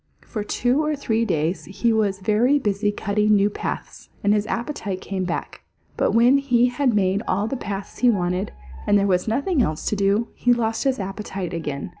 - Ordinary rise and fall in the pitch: Yes, average, 3.7 semitones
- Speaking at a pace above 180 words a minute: Yes, average, 195 wpm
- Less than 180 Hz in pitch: No, high, 210 Hz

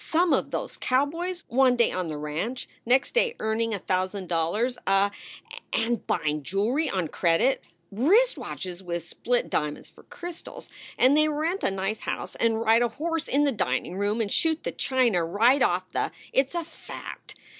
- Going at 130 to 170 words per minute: No, average, 185 wpm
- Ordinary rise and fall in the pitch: No, wide, 7.6 semitones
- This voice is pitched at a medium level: No, high, 230 Hz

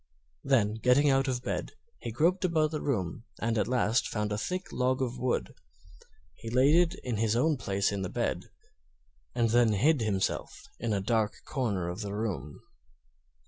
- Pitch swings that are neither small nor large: Yes, average, 4.4 semitones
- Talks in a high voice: No, low, 115 Hz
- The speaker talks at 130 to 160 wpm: No, average, 180 wpm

